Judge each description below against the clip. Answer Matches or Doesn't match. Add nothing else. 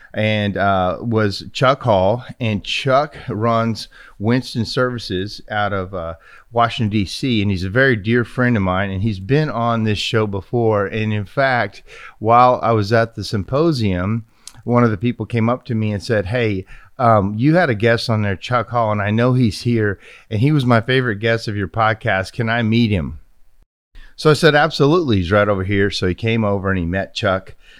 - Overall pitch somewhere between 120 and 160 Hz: Doesn't match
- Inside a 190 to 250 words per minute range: Matches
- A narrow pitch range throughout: Doesn't match